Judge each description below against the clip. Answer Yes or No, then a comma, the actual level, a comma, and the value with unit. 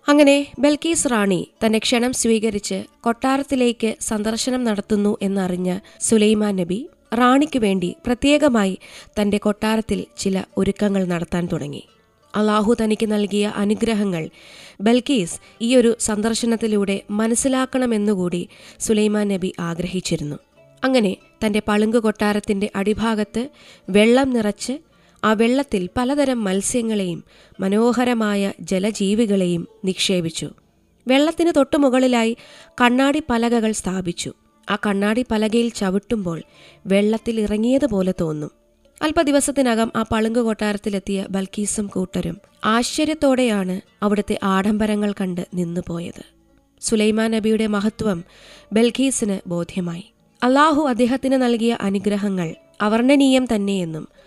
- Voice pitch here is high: Yes, high, 215 Hz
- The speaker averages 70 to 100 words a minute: Yes, average, 90 wpm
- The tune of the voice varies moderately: Yes, average, 3.7 semitones